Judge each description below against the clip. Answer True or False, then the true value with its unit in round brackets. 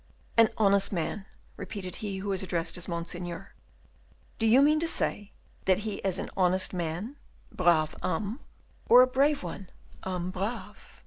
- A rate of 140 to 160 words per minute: True (155 wpm)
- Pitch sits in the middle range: False (195 Hz)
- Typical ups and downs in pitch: True (3.6 semitones)